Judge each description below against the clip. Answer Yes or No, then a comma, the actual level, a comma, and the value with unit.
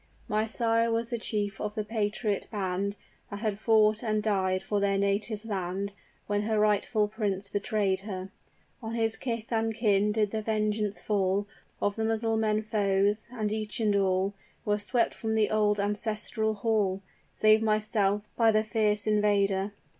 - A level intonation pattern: Yes, narrow, 1.6 semitones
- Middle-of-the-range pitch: No, high, 210 Hz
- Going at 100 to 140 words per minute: No, average, 160 wpm